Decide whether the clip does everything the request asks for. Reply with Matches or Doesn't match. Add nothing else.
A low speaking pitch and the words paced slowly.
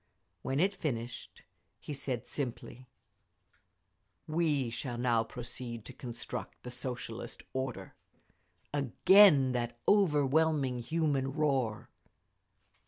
Matches